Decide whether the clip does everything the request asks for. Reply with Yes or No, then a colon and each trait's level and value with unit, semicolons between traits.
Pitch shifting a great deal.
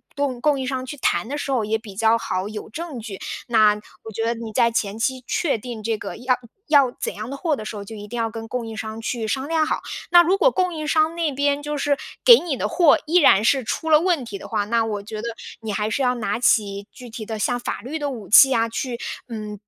No: average, 4.7 semitones